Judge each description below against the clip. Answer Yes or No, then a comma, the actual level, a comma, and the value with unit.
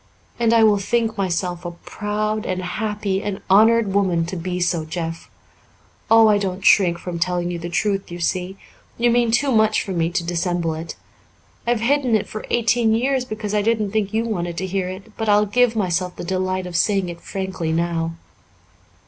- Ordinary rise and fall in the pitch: Yes, average, 3.7 semitones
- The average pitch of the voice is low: No, high, 195 Hz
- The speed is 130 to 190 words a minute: No, average, 200 wpm